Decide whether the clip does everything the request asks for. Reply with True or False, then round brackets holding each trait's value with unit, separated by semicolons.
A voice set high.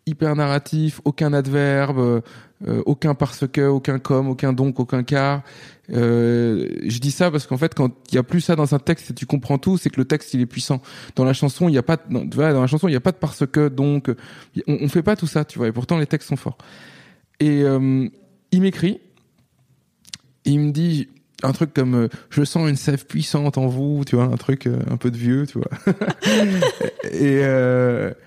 False (140 Hz)